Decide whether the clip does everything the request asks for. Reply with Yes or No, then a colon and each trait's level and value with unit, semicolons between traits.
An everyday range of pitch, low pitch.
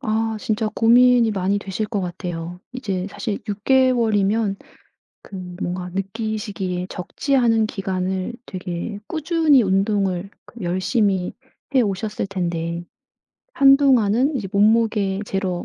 No: average, 3.4 semitones; high, 205 Hz